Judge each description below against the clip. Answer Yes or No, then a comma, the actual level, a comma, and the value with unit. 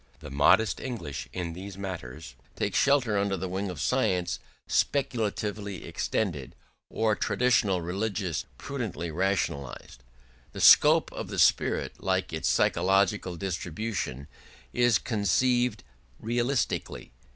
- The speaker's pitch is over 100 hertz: No, very low, 95 Hz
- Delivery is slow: Yes, slow, 110 wpm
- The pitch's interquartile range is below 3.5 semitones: No, average, 4.4 semitones